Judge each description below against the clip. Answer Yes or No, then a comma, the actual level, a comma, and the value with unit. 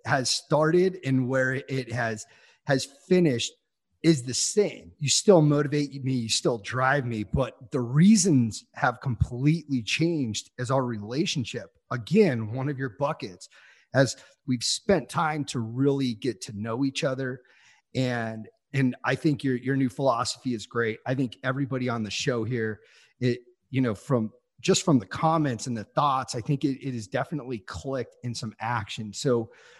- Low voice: Yes, low, 130 Hz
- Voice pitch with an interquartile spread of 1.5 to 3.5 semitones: Yes, average, 3.2 semitones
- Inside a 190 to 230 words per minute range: No, average, 165 wpm